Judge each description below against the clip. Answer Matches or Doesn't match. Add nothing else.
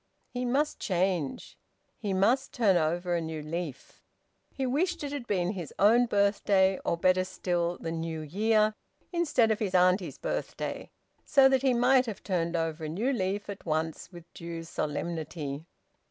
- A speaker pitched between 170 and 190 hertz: Matches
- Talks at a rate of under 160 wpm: Doesn't match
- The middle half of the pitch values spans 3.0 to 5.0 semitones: Doesn't match